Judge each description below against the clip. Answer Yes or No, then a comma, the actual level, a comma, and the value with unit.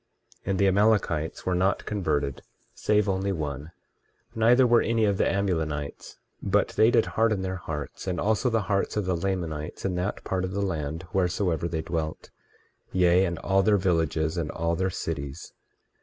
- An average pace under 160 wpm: No, average, 175 wpm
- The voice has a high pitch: No, very low, 95 Hz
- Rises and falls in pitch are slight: No, average, 3.7 semitones